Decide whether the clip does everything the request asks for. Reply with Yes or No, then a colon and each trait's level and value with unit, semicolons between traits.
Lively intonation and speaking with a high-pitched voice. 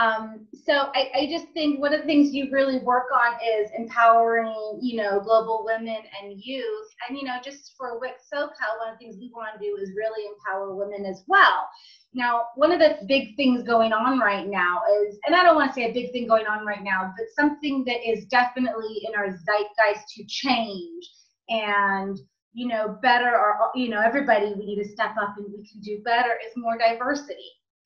No: average, 4.0 semitones; high, 230 Hz